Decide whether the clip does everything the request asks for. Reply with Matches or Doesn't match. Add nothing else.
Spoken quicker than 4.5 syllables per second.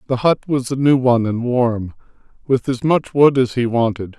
Matches